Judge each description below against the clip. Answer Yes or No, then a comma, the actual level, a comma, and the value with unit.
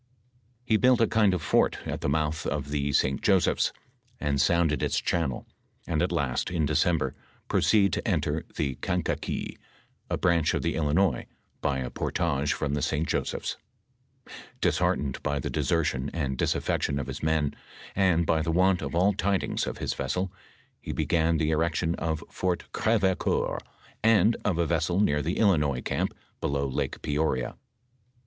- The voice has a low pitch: Yes, very low, 80 Hz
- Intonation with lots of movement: No, average, 3.8 semitones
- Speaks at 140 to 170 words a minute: Yes, average, 165 wpm